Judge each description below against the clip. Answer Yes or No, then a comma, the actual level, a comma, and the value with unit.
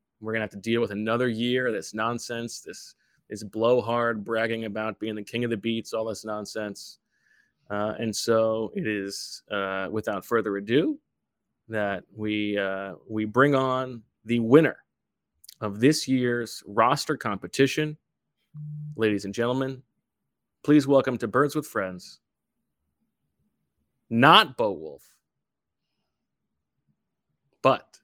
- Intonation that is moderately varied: Yes, average, 3.2 semitones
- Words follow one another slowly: Yes, slow, 130 wpm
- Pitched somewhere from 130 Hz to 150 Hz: No, low, 115 Hz